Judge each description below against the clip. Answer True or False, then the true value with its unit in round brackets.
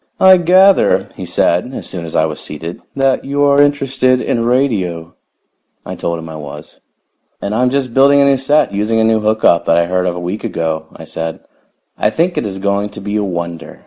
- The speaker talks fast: True (220 wpm)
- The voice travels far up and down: True (8.0 semitones)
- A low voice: True (105 Hz)